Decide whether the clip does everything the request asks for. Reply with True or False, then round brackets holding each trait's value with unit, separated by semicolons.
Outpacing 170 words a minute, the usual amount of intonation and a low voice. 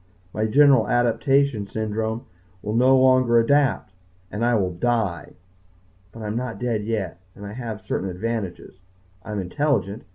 False (155 wpm; 3.2 semitones; 110 Hz)